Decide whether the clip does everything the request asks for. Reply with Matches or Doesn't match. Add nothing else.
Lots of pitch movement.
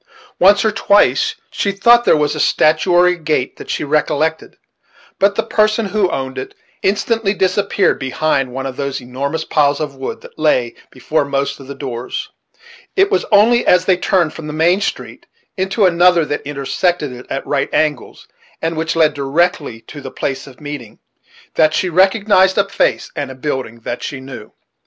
Matches